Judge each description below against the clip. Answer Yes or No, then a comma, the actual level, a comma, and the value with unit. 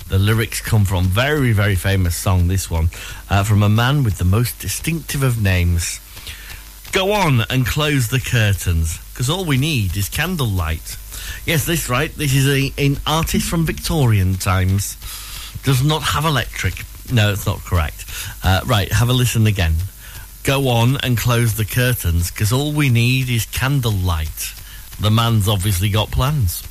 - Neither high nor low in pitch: No, low, 105 Hz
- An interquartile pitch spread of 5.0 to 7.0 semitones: Yes, wide, 5.5 semitones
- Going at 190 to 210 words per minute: No, average, 165 wpm